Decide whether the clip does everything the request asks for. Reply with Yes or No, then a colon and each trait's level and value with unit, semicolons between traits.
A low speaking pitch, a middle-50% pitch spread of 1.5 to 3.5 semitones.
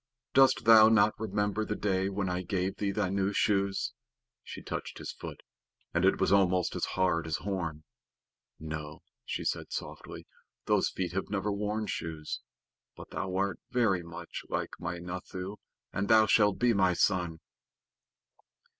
Yes: very low, 95 Hz; narrow, 2.6 semitones